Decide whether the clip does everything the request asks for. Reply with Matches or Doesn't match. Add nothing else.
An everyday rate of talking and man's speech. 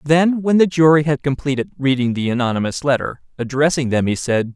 Matches